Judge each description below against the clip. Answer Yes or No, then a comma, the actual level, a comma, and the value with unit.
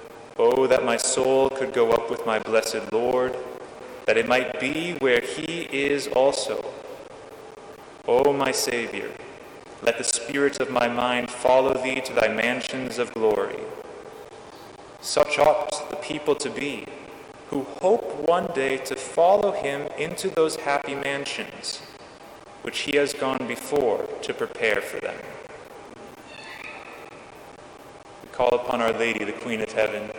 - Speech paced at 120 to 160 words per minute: Yes, average, 140 wpm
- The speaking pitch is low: No, medium, 150 Hz